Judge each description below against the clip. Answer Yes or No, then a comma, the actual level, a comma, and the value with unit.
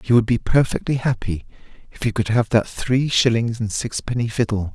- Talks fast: No, average, 190 wpm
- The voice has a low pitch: Yes, low, 115 Hz